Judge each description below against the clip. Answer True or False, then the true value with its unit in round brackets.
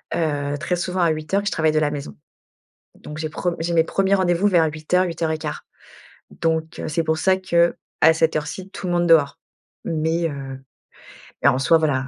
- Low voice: False (160 Hz)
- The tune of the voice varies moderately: False (2.2 semitones)